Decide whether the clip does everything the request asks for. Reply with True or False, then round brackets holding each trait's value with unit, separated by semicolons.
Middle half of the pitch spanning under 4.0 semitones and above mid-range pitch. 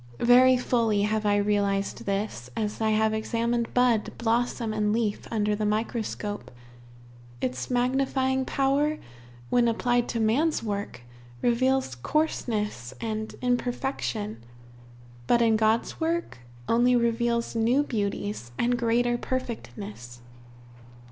True (2.8 semitones; 230 Hz)